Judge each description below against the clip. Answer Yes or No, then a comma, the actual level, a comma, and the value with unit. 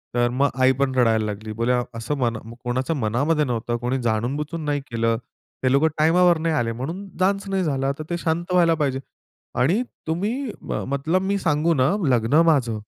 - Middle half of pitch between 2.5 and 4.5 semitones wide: No, wide, 5.5 semitones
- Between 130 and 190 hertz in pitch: Yes, medium, 140 Hz